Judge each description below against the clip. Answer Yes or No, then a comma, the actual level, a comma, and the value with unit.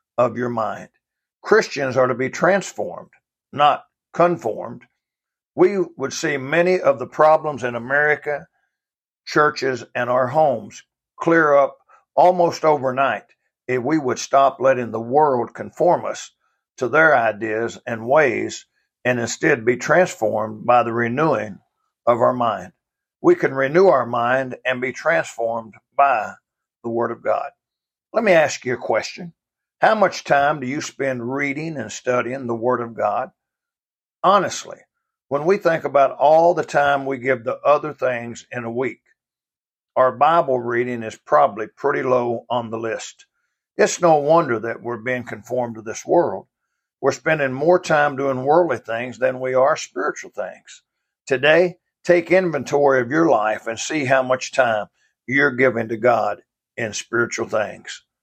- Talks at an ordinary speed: Yes, average, 155 wpm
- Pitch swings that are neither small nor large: Yes, average, 4.0 semitones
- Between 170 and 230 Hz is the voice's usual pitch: No, low, 130 Hz